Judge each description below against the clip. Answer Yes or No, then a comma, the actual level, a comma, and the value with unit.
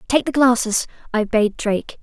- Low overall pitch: No, high, 235 Hz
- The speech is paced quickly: No, average, 180 wpm